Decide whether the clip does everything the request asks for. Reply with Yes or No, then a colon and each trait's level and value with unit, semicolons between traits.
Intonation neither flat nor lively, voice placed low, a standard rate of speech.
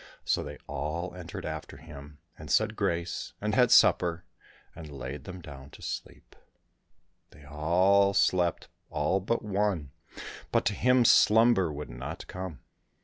Yes: average, 5.0 semitones; very low, 85 Hz; average, 145 wpm